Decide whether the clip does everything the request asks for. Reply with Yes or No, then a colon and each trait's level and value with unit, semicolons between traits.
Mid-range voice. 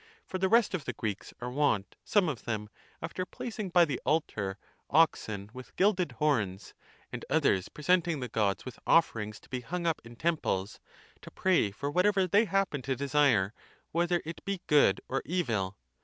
Yes: medium, 145 Hz